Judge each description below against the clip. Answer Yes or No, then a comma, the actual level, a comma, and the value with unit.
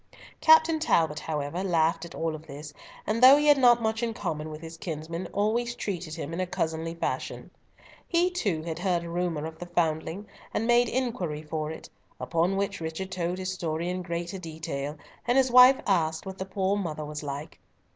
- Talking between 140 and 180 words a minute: No, average, 195 wpm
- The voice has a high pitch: No, medium, 175 Hz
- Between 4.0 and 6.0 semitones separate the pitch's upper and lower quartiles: Yes, average, 4.5 semitones